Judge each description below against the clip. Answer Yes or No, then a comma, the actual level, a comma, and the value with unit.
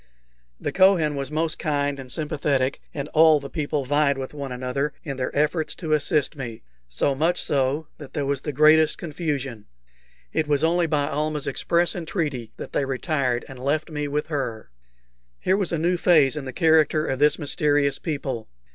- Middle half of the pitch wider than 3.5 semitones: No, narrow, 2.5 semitones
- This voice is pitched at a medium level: Yes, medium, 145 Hz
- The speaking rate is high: No, average, 180 wpm